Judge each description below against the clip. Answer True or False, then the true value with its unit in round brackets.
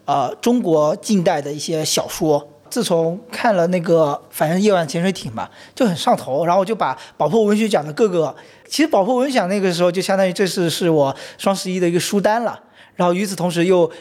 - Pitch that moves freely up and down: False (3.7 semitones)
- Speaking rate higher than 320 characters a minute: True (330 characters per minute)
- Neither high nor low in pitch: True (180 Hz)